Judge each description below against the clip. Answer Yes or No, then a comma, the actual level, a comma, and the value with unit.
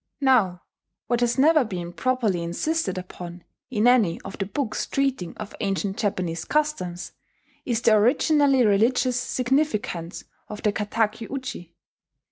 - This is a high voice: Yes, high, 215 Hz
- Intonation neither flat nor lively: No, wide, 5.8 semitones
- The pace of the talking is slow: Yes, slow, 130 wpm